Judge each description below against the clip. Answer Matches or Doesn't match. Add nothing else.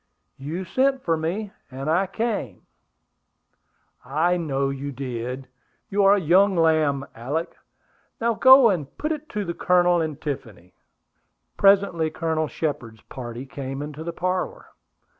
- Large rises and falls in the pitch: Matches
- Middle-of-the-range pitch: Matches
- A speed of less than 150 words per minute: Matches